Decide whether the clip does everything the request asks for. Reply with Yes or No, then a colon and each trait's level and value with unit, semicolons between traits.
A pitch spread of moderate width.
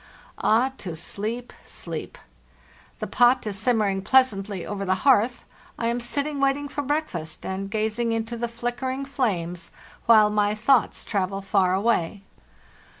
Yes: average, 4.0 semitones